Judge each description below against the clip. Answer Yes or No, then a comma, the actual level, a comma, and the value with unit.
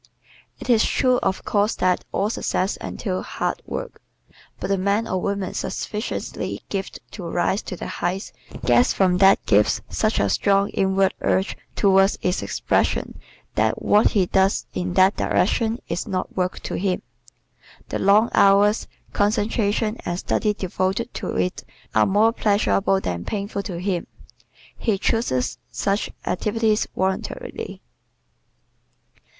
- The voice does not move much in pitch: Yes, narrow, 2.2 semitones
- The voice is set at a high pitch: Yes, high, 195 Hz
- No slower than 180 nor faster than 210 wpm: No, average, 140 wpm